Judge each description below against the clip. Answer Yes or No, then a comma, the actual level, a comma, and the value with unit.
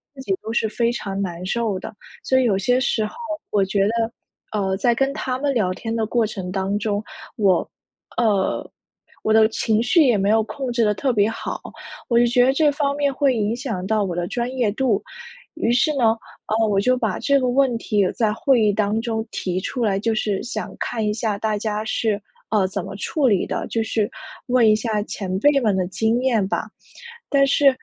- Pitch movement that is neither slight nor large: Yes, average, 3.3 semitones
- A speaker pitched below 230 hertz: Yes, high, 220 Hz